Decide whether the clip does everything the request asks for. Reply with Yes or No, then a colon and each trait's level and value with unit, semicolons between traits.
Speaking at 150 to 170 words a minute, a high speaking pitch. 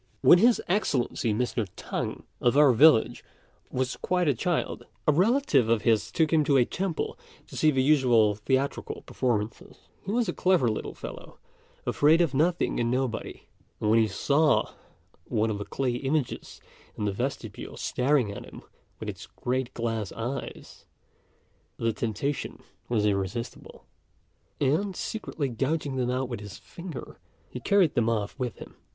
No: average, 160 wpm; low, 130 Hz